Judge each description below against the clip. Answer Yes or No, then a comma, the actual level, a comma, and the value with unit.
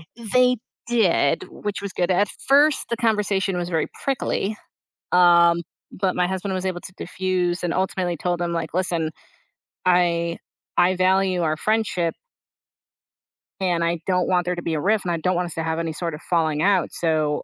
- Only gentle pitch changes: Yes, narrow, 2.1 semitones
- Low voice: No, medium, 180 Hz